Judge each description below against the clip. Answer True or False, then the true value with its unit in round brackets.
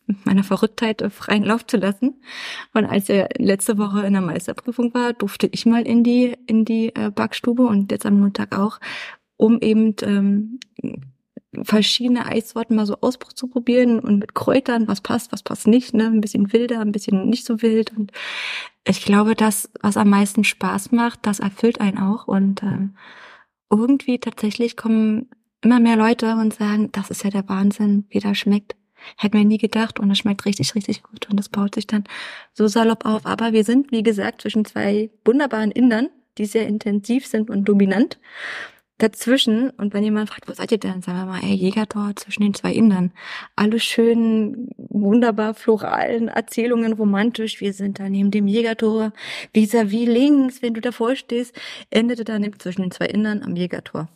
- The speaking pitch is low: False (220 Hz)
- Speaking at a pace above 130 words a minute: True (180 wpm)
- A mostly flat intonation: True (2.3 semitones)